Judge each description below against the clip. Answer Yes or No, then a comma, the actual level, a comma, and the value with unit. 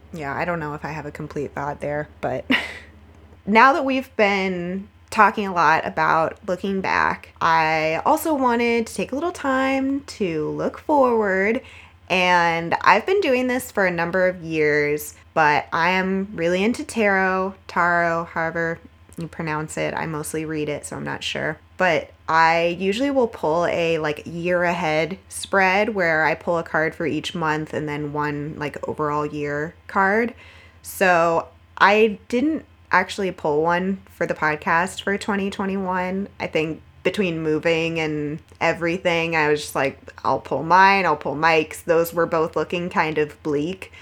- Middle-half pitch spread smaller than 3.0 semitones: No, average, 4.0 semitones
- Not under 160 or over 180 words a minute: Yes, average, 165 wpm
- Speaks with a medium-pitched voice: Yes, medium, 170 Hz